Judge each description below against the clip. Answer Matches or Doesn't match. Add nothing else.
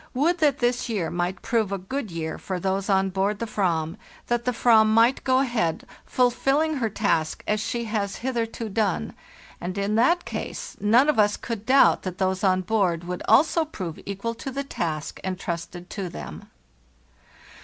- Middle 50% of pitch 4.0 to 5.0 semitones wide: Matches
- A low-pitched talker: Doesn't match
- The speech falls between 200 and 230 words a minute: Doesn't match